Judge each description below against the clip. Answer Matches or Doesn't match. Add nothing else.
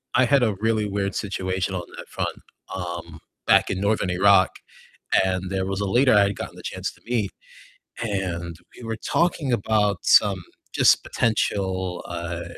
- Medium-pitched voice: Doesn't match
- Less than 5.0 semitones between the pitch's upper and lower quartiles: Matches